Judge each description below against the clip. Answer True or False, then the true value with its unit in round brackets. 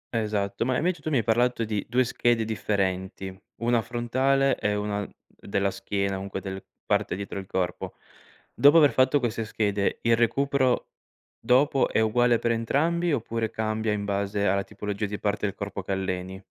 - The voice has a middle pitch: False (110 Hz)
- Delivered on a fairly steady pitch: False (3.7 semitones)